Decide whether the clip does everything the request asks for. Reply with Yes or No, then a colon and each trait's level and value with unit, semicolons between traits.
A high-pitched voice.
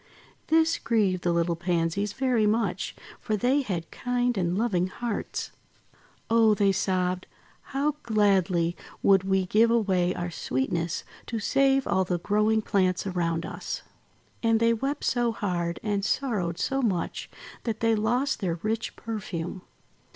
Yes: high, 205 Hz